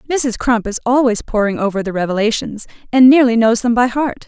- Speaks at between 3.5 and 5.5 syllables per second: No, 5.8 syllables/s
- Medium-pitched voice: No, high, 235 Hz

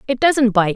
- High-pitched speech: Yes, high, 245 Hz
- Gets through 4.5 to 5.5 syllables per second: Yes, 4.7 syllables/s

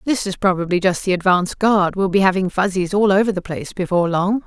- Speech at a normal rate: No, fast, 230 wpm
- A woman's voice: Yes, female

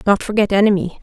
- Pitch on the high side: Yes, high, 200 Hz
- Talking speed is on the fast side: No, average, 175 wpm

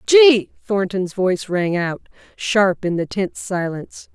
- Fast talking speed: No, average, 145 wpm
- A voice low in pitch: No, high, 190 Hz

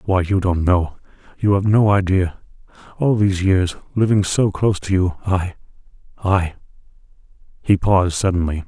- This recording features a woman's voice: No, male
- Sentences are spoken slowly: Yes, slow, 120 wpm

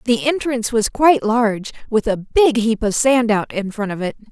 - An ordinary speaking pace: No, fast, 225 wpm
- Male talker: No, female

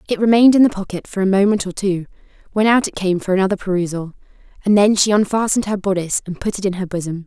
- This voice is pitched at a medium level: No, high, 195 Hz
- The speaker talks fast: Yes, fast, 240 wpm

